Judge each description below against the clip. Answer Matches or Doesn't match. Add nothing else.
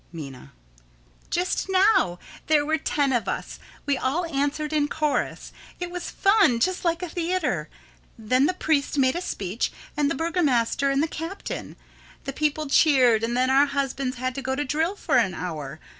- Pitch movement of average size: Matches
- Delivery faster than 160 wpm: Matches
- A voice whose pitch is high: Matches